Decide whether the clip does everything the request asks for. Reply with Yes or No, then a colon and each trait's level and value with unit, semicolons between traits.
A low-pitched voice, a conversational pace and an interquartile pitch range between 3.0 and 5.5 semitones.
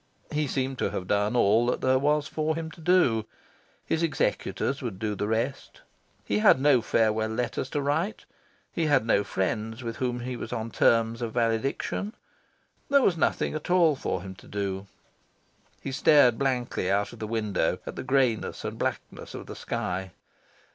Yes: low, 120 Hz; average, 180 wpm; average, 4.8 semitones